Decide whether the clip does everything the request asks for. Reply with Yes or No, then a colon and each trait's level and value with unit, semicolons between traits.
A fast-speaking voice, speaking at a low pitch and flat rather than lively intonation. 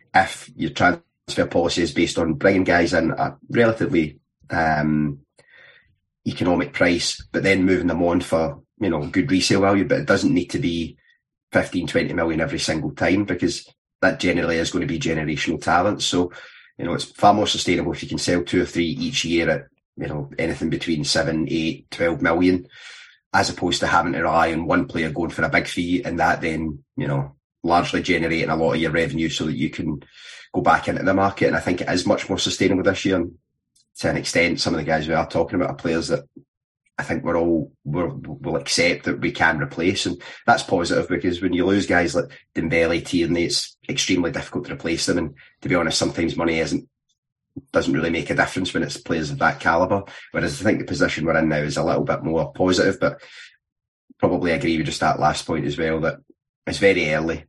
Yes: fast, 215 wpm; very low, 85 Hz; narrow, 1.9 semitones